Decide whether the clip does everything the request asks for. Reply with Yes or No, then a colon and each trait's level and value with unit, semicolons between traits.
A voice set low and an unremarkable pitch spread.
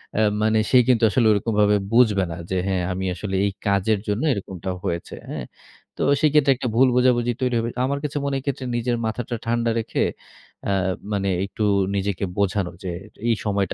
Yes: low, 110 Hz; average, 3.8 semitones